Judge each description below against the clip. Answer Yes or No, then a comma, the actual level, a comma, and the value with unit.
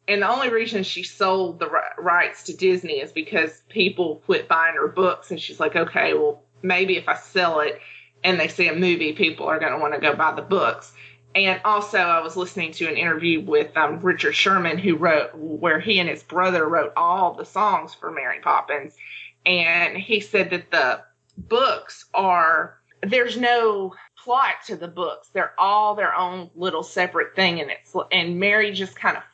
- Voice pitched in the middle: Yes, medium, 180 Hz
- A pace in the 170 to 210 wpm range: Yes, average, 195 wpm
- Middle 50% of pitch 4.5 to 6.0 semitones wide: No, average, 3.6 semitones